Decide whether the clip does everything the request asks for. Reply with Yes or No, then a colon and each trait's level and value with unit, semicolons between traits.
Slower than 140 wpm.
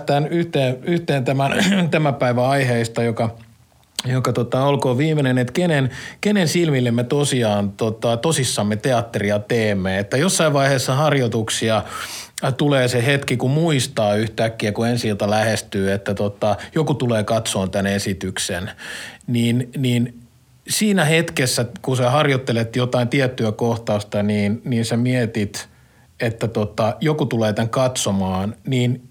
Yes: average, 130 wpm